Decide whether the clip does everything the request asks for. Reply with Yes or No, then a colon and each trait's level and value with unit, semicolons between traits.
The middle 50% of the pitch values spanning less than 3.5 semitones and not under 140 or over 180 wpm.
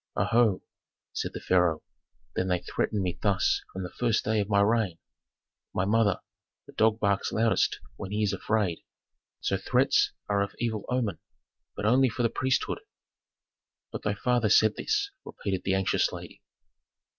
Yes: average, 2.8 semitones; average, 165 wpm